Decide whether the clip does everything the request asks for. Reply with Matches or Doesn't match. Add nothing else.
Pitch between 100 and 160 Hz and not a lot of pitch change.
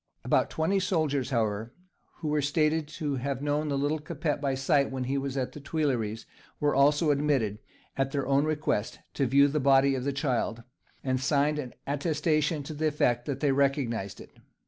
Matches